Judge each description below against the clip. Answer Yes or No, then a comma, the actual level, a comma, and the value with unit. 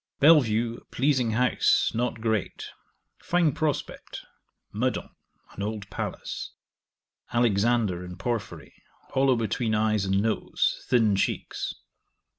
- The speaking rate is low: Yes, slow, 105 wpm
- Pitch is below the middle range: Yes, low, 115 Hz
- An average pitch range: Yes, average, 3.0 semitones